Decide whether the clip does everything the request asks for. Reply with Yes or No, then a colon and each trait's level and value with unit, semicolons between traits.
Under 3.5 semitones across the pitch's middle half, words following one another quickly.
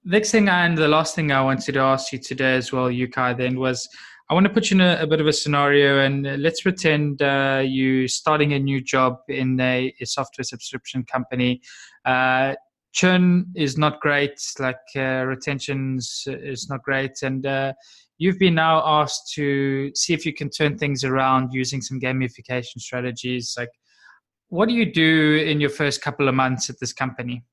No: average, 2.8 semitones; average, 190 wpm